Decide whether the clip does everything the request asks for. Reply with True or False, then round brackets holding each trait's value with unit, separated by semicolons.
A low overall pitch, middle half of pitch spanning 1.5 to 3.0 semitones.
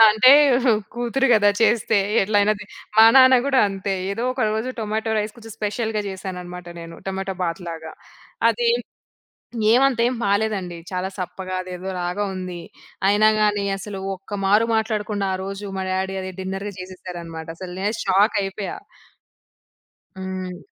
False (195 Hz; 2.6 semitones)